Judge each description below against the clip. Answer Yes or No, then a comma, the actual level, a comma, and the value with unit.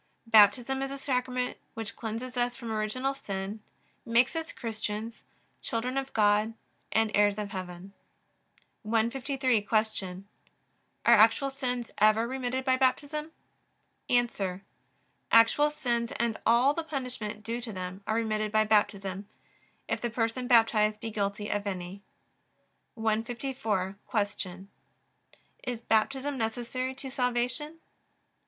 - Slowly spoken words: Yes, slow, 120 wpm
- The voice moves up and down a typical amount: Yes, average, 3.2 semitones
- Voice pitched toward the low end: No, high, 230 Hz